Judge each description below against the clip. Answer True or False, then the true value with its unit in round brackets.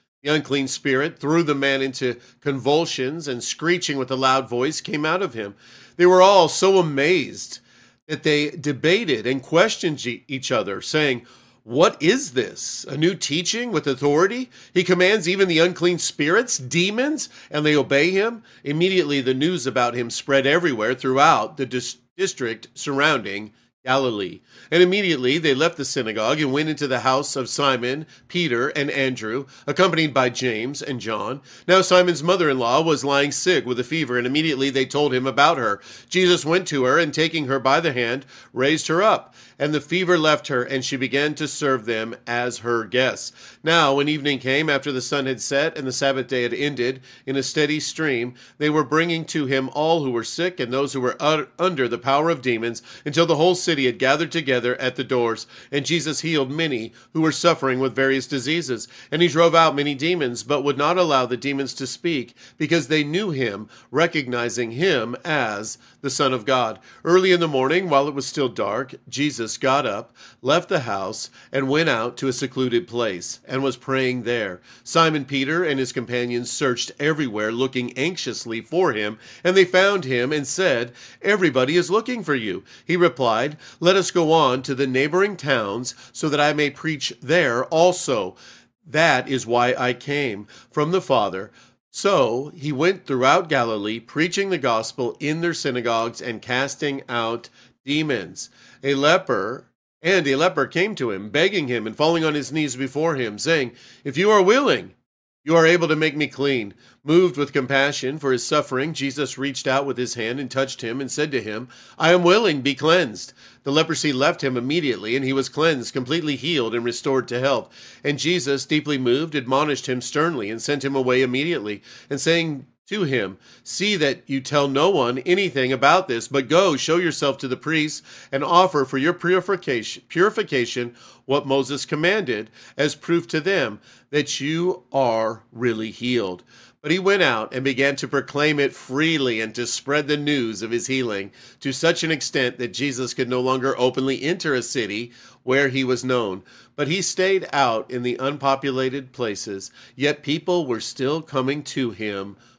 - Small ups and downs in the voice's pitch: False (4.0 semitones)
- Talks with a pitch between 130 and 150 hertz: True (140 Hz)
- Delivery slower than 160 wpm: False (185 wpm)